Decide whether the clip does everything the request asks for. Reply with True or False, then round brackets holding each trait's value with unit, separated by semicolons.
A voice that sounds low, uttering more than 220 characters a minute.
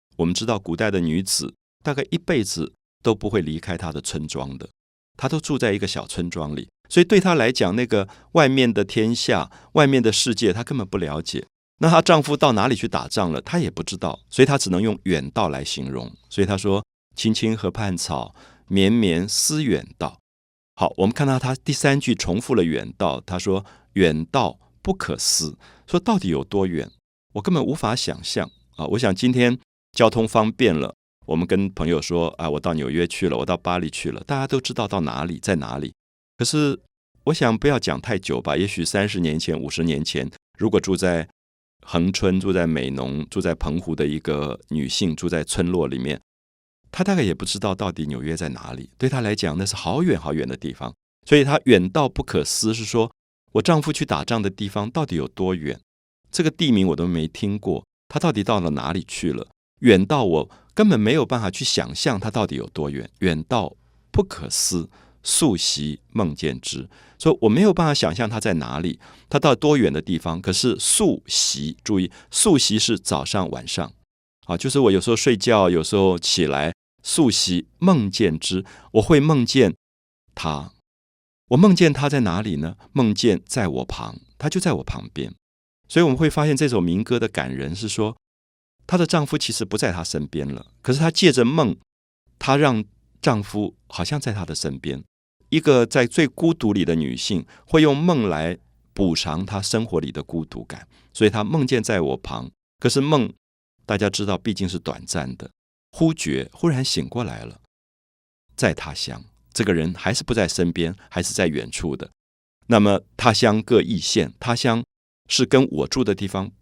True (100 Hz; 270 characters per minute)